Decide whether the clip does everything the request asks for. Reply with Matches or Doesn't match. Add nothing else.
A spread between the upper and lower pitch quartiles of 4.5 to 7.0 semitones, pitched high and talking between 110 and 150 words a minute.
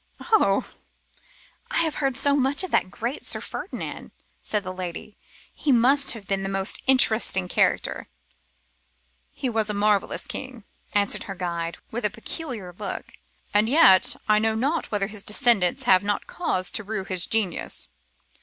Doesn't match